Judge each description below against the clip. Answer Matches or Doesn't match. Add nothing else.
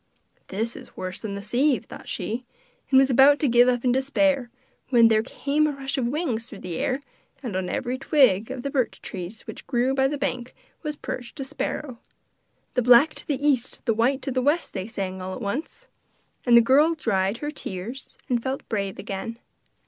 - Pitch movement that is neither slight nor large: Matches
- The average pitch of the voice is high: Matches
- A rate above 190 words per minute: Matches